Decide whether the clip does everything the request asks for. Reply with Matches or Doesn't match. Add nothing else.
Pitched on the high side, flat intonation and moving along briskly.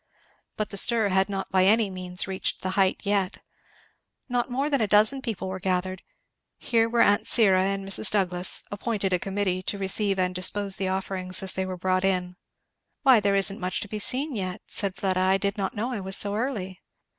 Matches